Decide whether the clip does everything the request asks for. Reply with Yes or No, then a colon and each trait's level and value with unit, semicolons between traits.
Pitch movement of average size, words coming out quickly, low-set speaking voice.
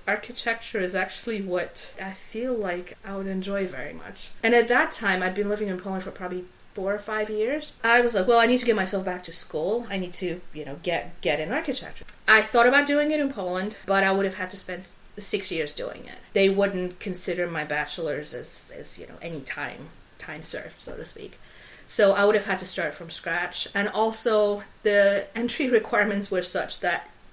No: average, 3.2 semitones; fast, 215 wpm; high, 200 Hz